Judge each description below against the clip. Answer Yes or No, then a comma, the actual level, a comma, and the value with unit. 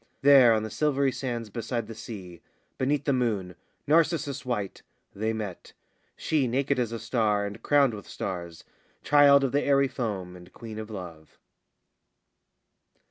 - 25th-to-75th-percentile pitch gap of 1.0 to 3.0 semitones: No, average, 5.1 semitones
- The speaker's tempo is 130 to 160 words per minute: Yes, average, 150 wpm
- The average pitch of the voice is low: Yes, low, 115 Hz